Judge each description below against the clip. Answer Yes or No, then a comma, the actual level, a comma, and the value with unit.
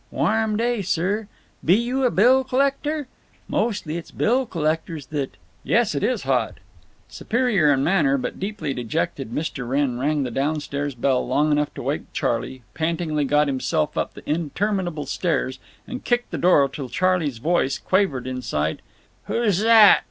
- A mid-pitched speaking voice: Yes, medium, 160 Hz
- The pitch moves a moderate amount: No, wide, 7.2 semitones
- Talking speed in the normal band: Yes, average, 160 wpm